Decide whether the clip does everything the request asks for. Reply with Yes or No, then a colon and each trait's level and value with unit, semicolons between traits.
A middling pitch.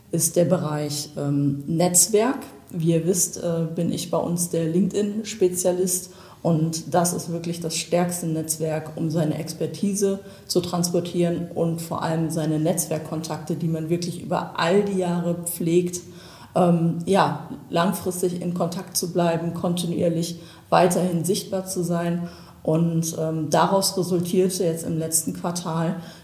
Yes: medium, 170 Hz